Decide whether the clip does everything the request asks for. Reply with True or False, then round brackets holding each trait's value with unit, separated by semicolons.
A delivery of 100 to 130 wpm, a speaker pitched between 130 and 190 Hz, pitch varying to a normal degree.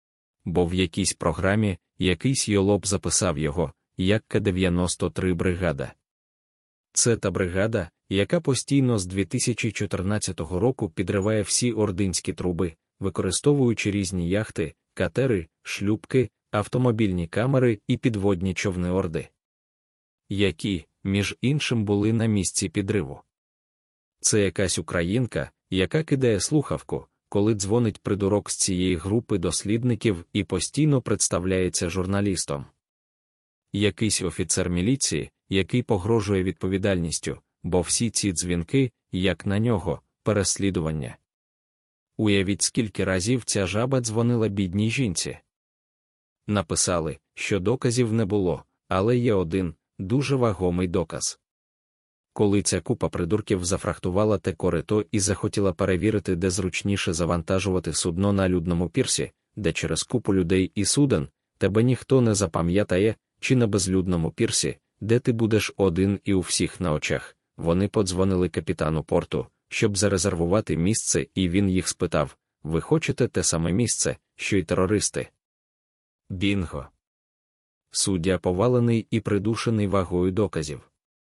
False (115 wpm; 100 Hz; 3.3 semitones)